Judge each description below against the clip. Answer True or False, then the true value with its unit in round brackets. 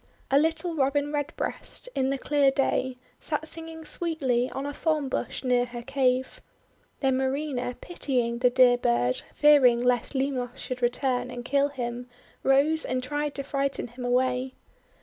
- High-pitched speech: True (265 Hz)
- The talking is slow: False (155 wpm)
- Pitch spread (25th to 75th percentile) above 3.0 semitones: False (2.6 semitones)